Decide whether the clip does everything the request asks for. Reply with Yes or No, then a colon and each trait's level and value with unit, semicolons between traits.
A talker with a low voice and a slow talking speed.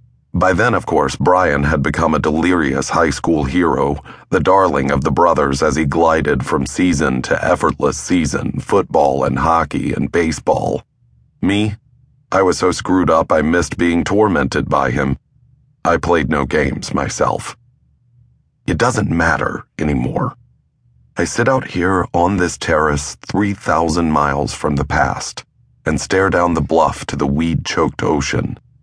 No: very low, 80 Hz; average, 150 wpm